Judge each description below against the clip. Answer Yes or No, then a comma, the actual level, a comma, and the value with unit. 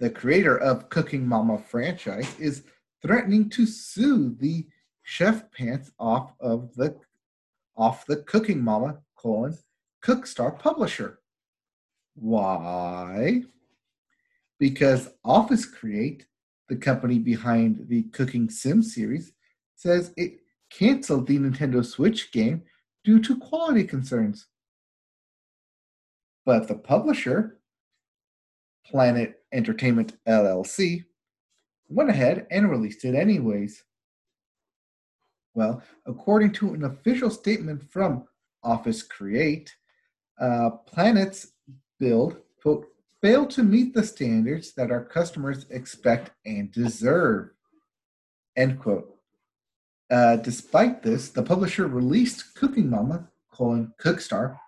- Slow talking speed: Yes, slow, 100 wpm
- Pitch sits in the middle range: Yes, medium, 145 Hz